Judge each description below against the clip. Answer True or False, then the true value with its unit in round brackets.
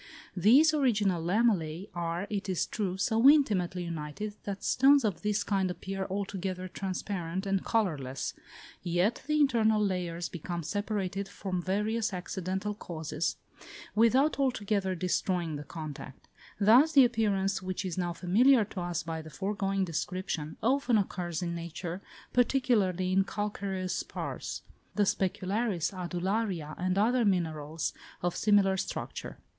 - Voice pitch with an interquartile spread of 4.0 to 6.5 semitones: False (3.3 semitones)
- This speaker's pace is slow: True (130 wpm)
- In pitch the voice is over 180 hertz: True (190 Hz)